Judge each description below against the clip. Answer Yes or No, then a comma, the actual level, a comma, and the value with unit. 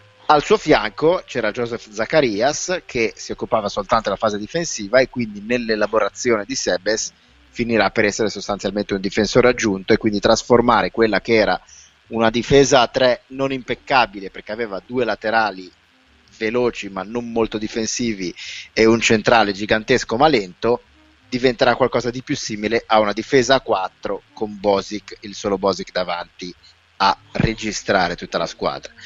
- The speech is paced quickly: No, average, 150 wpm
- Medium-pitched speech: No, low, 110 Hz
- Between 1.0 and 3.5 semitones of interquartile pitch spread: Yes, average, 3.0 semitones